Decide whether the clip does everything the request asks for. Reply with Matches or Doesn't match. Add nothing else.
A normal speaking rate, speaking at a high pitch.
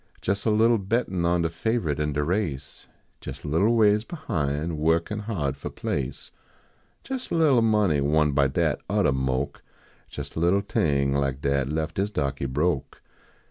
Doesn't match